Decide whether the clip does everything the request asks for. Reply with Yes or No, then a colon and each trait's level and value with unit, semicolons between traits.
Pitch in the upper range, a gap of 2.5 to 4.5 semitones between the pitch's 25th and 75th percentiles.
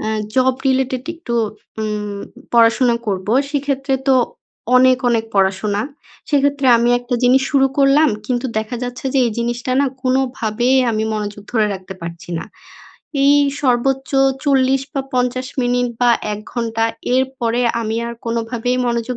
Yes: high, 245 Hz; average, 2.8 semitones